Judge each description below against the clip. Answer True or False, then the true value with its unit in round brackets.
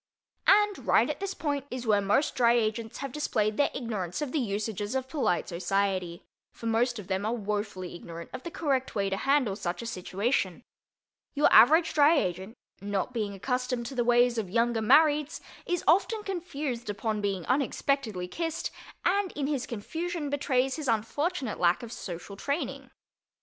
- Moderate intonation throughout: False (6.0 semitones)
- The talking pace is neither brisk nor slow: True (170 wpm)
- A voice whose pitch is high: True (240 Hz)